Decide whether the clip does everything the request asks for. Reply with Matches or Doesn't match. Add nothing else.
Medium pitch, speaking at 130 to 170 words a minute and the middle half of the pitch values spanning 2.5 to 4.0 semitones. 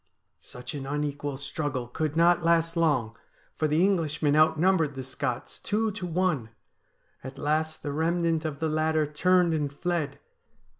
Matches